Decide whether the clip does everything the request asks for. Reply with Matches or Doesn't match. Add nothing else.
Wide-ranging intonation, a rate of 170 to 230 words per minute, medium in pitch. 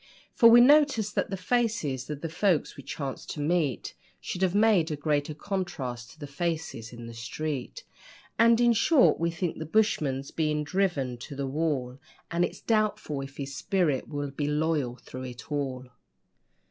Matches